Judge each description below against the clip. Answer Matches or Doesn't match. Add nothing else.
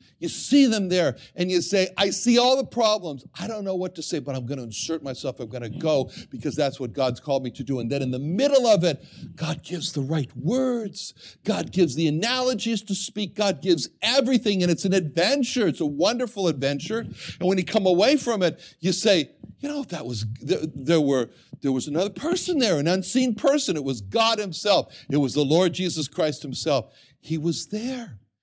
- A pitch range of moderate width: Doesn't match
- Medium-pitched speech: Matches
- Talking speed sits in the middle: Doesn't match